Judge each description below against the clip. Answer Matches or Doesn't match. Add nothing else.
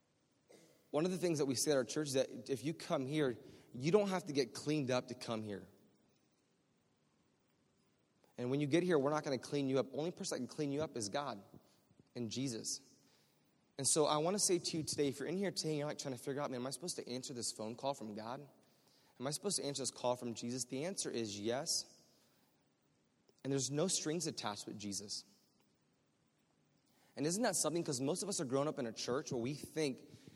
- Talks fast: Matches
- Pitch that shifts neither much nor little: Matches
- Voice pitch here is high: Doesn't match